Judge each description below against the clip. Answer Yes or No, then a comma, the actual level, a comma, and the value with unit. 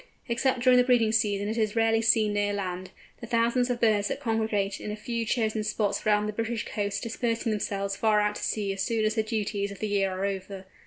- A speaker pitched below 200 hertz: No, high, 215 Hz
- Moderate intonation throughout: No, narrow, 2.0 semitones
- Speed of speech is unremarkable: No, fast, 230 wpm